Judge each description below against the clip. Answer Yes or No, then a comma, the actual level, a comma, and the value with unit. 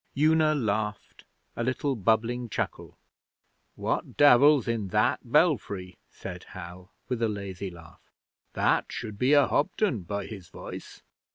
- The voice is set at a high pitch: No, low, 110 Hz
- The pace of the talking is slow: Yes, slow, 130 wpm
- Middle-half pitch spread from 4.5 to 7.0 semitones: Yes, wide, 5.5 semitones